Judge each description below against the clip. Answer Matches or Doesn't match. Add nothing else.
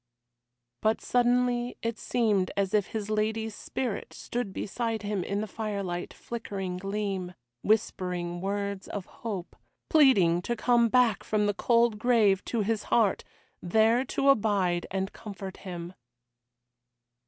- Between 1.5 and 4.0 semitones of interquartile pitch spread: Matches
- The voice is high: Matches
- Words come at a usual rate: Doesn't match